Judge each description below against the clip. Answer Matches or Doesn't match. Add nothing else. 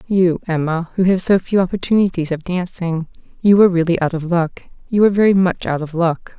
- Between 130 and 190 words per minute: Doesn't match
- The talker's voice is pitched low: Doesn't match